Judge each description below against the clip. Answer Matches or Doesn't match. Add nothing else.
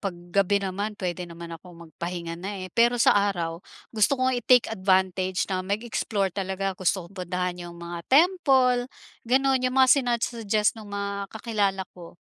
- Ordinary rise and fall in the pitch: Matches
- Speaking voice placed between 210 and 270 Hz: Doesn't match